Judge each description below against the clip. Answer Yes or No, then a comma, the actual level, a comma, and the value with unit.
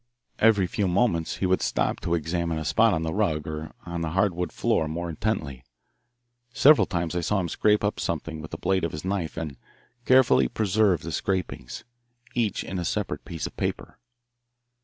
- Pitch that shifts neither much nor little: Yes, average, 4.0 semitones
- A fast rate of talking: No, average, 185 wpm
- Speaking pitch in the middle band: No, very low, 85 Hz